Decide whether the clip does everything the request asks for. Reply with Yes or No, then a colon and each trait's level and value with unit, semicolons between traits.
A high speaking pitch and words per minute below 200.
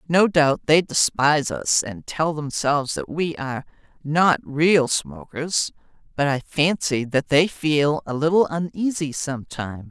No: medium, 150 Hz; average, 145 wpm